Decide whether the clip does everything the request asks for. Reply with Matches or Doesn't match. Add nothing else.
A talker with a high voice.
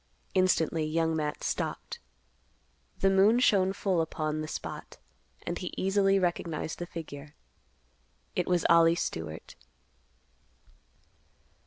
Doesn't match